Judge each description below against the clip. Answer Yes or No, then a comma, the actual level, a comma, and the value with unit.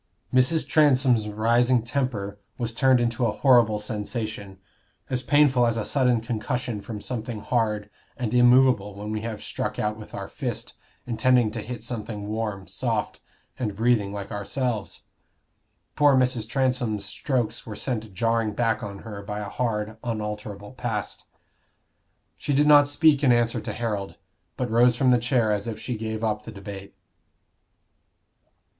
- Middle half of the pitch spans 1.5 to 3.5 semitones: Yes, average, 3.0 semitones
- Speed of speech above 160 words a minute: No, average, 155 wpm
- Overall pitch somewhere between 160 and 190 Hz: No, low, 115 Hz